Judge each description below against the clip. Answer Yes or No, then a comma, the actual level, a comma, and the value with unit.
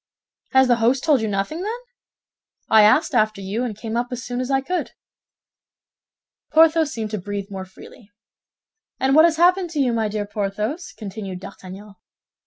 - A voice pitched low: No, high, 230 Hz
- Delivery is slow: No, average, 175 wpm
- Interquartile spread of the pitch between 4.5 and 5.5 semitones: Yes, average, 5.2 semitones